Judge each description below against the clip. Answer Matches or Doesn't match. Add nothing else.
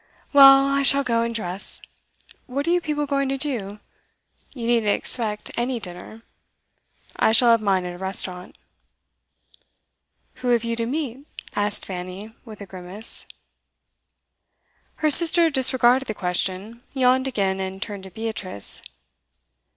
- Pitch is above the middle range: Matches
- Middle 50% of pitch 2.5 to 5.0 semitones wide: Doesn't match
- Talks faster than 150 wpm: Doesn't match